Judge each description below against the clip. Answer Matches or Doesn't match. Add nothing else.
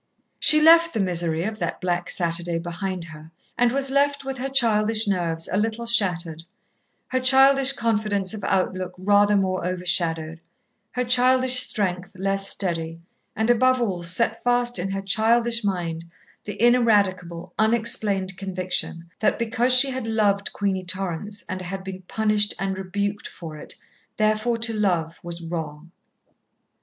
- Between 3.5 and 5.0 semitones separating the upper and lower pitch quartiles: Matches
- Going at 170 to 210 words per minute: Doesn't match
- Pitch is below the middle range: Doesn't match